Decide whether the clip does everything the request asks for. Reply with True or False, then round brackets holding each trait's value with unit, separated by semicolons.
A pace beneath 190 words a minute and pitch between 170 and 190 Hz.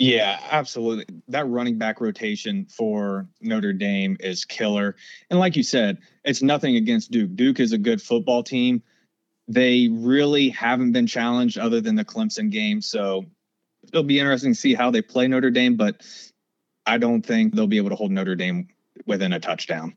True (180 wpm; 185 Hz)